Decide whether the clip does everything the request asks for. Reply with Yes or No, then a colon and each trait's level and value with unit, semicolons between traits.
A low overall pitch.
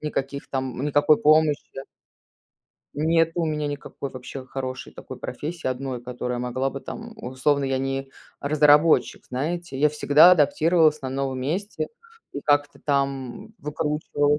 No: medium, 145 Hz